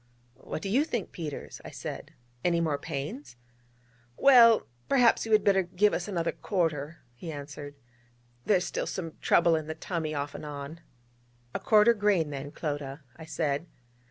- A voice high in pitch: No, medium, 165 Hz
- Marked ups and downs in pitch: Yes, wide, 5.7 semitones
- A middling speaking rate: Yes, average, 160 wpm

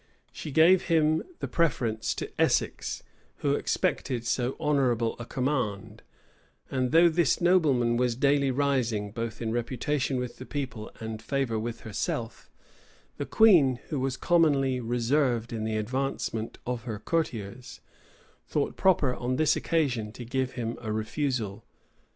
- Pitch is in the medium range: No, low, 125 Hz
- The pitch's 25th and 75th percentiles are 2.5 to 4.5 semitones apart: Yes, average, 3.8 semitones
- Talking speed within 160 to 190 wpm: No, average, 140 wpm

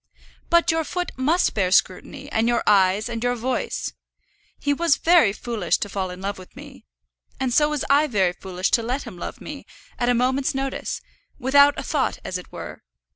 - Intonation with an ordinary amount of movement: No, wide, 6.2 semitones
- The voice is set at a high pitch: Yes, high, 245 Hz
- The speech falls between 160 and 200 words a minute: Yes, average, 195 wpm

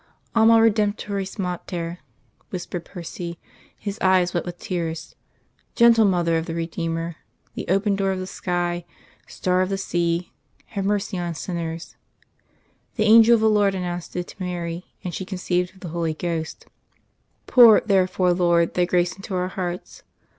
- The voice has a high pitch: No, medium, 180 Hz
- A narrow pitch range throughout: Yes, narrow, 2.3 semitones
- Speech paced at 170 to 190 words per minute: No, average, 155 wpm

